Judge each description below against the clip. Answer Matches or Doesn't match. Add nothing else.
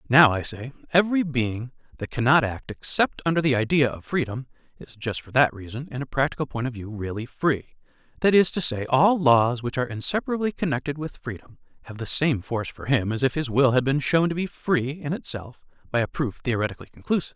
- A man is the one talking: Matches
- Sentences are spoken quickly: Matches